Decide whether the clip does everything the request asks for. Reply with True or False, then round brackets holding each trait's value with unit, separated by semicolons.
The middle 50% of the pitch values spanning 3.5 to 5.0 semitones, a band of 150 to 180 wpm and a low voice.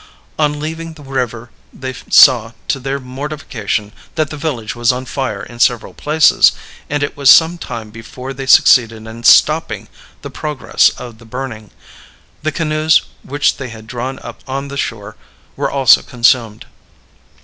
True (3.8 semitones; 160 wpm; 130 Hz)